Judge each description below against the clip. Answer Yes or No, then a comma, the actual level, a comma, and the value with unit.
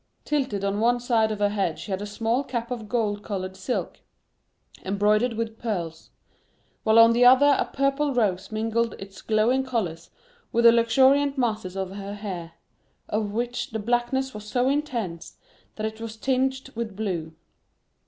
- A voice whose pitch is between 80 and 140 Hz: No, high, 220 Hz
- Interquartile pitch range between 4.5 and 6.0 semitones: No, average, 3.3 semitones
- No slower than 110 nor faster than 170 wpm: Yes, average, 165 wpm